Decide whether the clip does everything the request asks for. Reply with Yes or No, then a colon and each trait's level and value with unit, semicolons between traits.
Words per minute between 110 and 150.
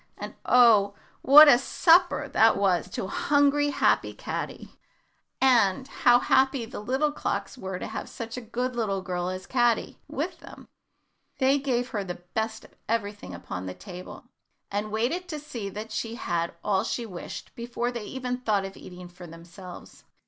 No: average, 170 wpm